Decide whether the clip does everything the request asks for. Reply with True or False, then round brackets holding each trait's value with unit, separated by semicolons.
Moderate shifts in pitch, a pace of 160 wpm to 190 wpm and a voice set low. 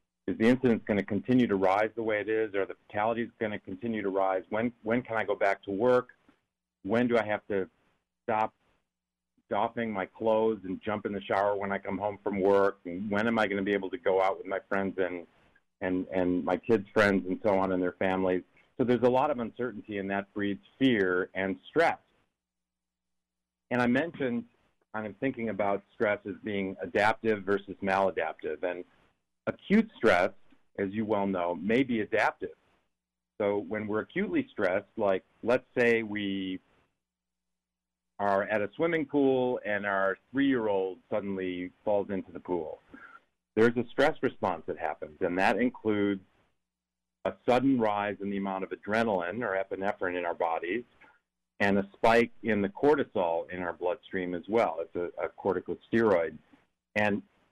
True (3.3 semitones; 175 wpm; 100 Hz)